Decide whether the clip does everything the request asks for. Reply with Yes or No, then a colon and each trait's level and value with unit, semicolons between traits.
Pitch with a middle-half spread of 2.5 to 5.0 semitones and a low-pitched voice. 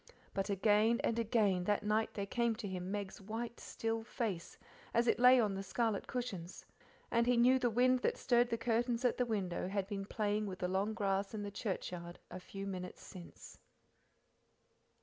No: average, 3.2 semitones; high, 210 Hz